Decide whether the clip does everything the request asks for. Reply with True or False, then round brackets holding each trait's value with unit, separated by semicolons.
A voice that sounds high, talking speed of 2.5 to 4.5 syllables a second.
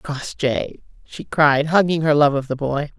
False (145 Hz; 4.1 syllables/s)